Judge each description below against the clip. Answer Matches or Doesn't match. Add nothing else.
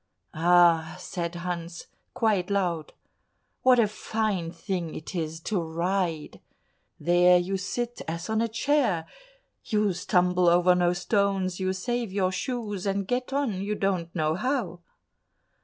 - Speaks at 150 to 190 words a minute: Doesn't match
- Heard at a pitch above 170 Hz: Matches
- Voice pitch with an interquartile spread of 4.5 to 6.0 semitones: Doesn't match